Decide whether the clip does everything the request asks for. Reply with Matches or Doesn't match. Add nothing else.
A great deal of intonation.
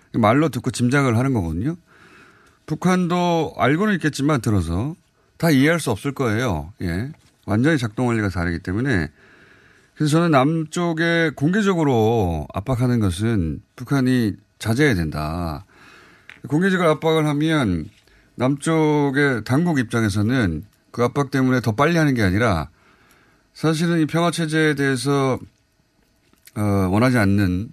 Matches